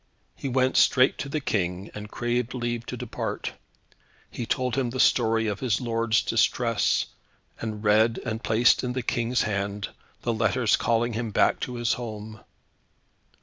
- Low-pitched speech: Yes, low, 115 Hz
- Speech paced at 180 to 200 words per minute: No, average, 160 wpm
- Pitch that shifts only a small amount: Yes, narrow, 2.3 semitones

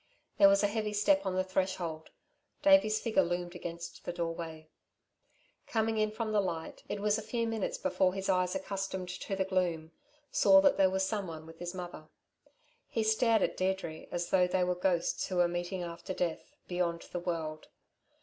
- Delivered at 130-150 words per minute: No, average, 185 wpm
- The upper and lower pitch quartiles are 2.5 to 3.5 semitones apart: Yes, average, 3.1 semitones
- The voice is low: No, medium, 185 Hz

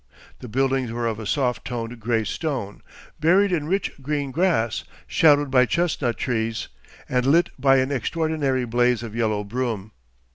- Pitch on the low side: Yes, low, 125 Hz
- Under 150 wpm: No, average, 155 wpm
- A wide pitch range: No, average, 4.1 semitones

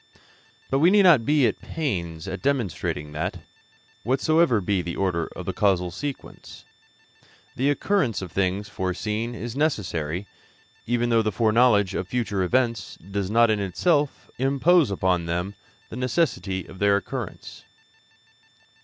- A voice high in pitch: No, low, 105 Hz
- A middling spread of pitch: No, wide, 6.1 semitones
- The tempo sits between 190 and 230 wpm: No, average, 145 wpm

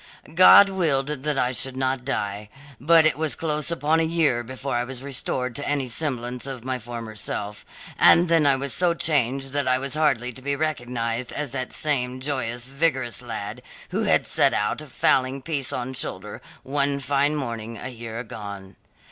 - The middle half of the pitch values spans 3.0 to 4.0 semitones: Yes, average, 3.3 semitones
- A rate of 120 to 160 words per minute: No, average, 180 wpm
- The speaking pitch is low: Yes, low, 130 Hz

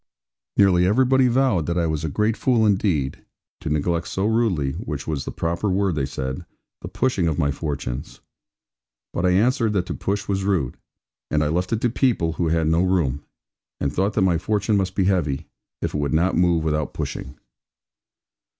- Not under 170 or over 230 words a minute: Yes, average, 190 wpm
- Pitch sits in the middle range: No, very low, 90 Hz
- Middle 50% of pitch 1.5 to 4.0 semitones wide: No, average, 4.9 semitones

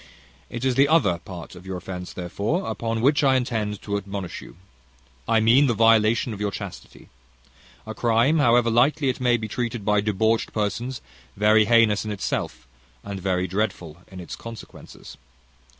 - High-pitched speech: No, low, 110 Hz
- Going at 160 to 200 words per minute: Yes, average, 165 wpm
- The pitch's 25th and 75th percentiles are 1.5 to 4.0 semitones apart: Yes, average, 3.4 semitones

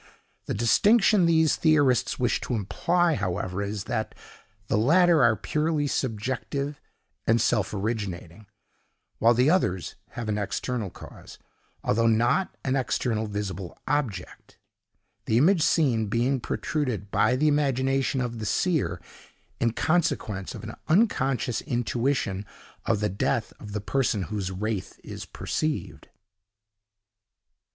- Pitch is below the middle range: Yes, low, 120 Hz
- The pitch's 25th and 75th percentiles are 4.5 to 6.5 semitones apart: Yes, wide, 5.5 semitones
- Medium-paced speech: No, slow, 125 wpm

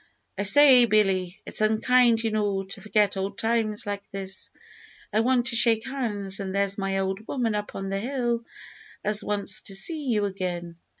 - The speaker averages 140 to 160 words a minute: No, average, 180 wpm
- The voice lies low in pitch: No, high, 210 Hz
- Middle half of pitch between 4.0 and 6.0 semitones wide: No, average, 3.2 semitones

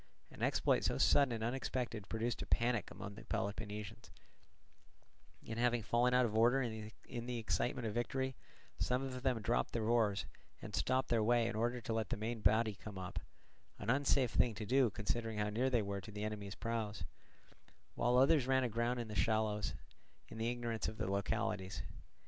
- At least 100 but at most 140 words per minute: No, average, 185 wpm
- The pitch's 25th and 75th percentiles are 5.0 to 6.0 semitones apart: No, narrow, 2.5 semitones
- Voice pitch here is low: Yes, low, 115 Hz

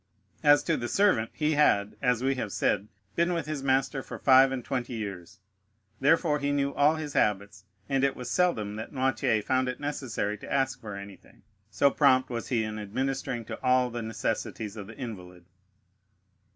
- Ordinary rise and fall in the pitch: Yes, average, 4.4 semitones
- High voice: No, low, 125 Hz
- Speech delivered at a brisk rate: No, average, 185 wpm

